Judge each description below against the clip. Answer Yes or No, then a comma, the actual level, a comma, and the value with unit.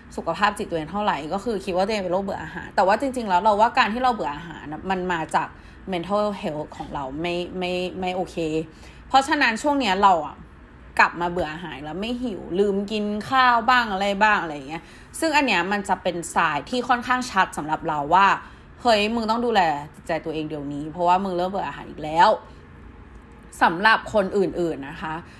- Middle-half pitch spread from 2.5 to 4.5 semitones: No, average, 5.0 semitones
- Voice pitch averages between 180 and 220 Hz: Yes, medium, 185 Hz